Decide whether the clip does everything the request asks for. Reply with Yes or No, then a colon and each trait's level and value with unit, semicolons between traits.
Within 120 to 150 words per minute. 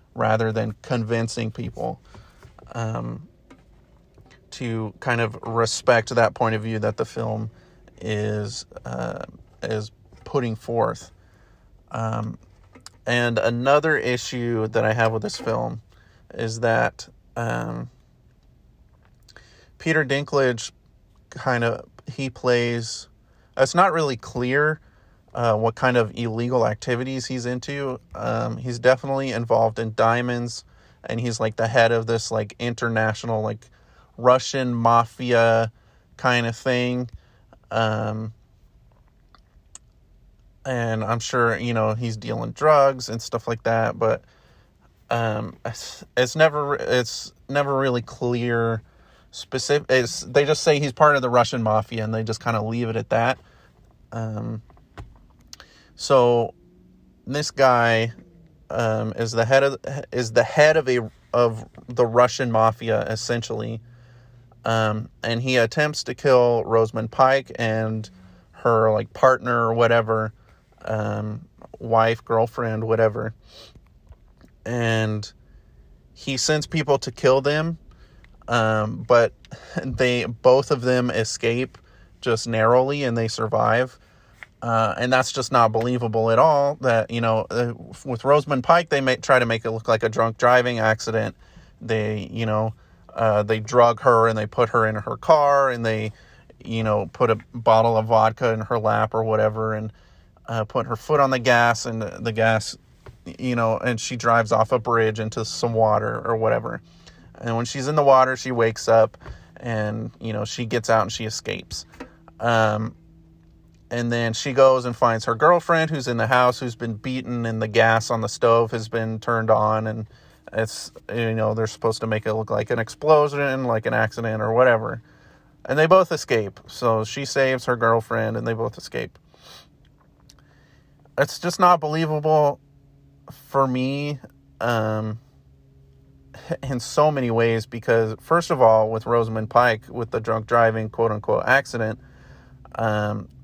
Yes: average, 145 wpm